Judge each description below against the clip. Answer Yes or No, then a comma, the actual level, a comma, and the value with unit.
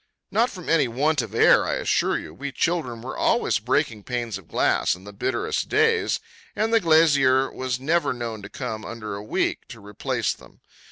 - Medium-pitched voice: No, low, 125 Hz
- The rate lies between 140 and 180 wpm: No, average, 190 wpm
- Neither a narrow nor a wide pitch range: No, wide, 6.6 semitones